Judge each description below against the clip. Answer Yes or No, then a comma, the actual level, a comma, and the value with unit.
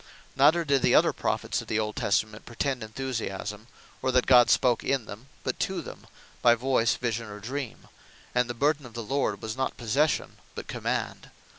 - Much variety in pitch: No, average, 3.4 semitones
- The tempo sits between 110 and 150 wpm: No, average, 185 wpm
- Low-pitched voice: Yes, low, 120 Hz